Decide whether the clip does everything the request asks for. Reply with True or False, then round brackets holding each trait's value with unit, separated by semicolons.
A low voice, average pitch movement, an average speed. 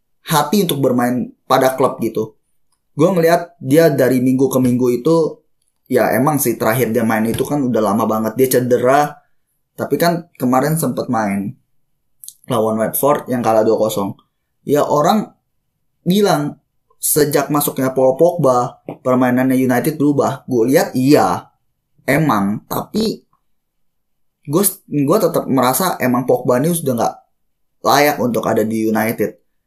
True (130 Hz; 4.2 semitones; 130 wpm)